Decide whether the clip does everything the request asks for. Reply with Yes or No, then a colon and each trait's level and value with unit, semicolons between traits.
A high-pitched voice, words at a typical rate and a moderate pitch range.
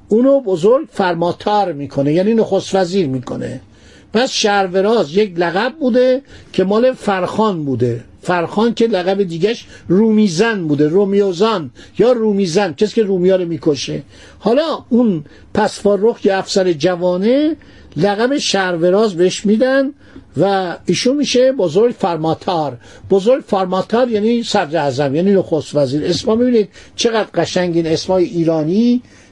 Yes: high, 195 Hz; average, 125 wpm; average, 4.7 semitones